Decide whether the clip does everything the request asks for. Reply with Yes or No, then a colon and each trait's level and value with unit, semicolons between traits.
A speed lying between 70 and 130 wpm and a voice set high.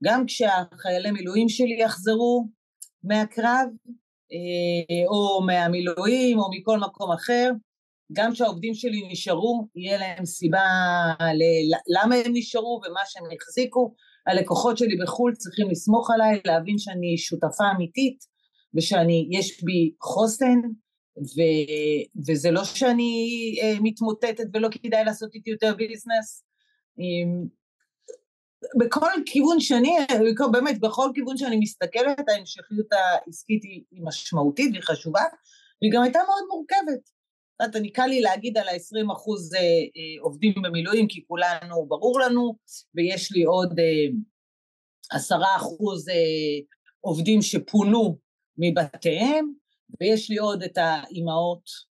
Yes: average, 110 wpm; high, 215 Hz